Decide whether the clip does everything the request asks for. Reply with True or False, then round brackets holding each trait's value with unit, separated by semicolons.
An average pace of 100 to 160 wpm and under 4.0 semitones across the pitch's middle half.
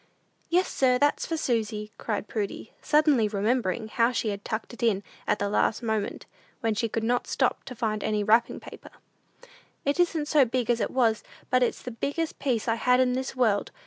False (200 wpm; 3.0 semitones)